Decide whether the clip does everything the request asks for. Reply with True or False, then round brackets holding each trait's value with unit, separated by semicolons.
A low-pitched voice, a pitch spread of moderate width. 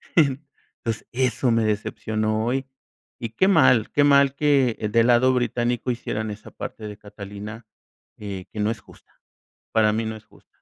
True (115 Hz; 3.2 semitones)